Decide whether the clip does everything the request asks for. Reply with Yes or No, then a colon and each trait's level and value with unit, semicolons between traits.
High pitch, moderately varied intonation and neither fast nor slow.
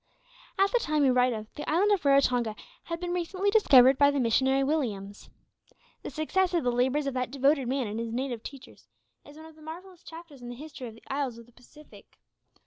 No: very high, 275 Hz; average, 4.4 semitones; fast, 225 wpm